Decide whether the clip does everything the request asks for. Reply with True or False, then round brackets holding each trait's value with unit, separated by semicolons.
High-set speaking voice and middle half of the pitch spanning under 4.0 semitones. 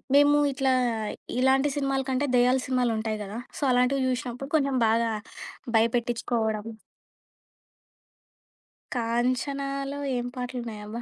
True (250 Hz; 2.9 semitones)